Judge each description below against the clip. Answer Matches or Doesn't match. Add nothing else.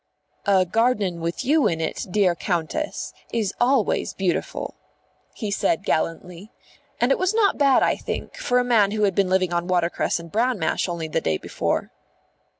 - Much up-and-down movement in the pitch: Matches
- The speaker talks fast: Doesn't match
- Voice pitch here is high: Matches